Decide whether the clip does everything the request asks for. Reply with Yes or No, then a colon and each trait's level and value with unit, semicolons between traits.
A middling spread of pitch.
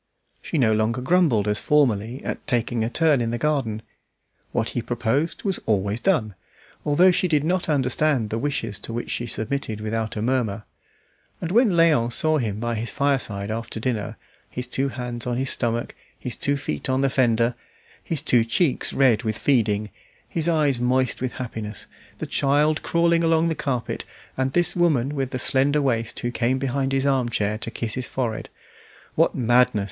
Yes: average, 4.0 semitones